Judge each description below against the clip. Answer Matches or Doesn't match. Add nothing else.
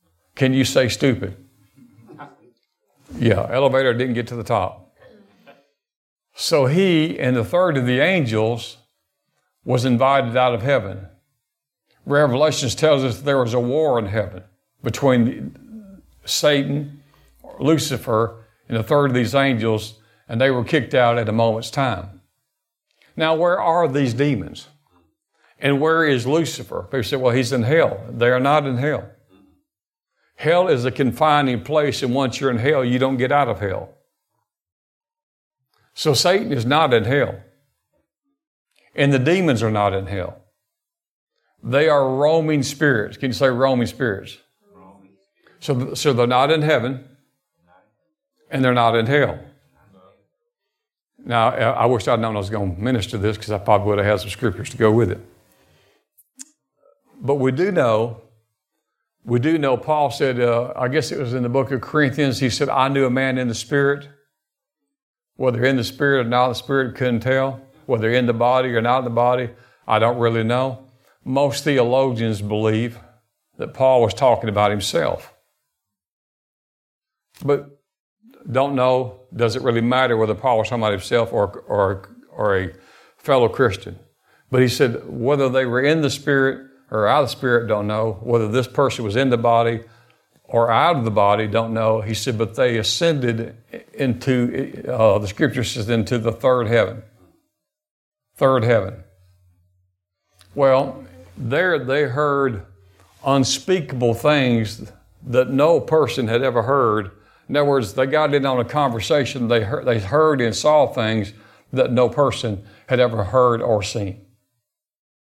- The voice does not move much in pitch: Doesn't match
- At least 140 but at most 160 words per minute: Matches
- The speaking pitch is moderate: Doesn't match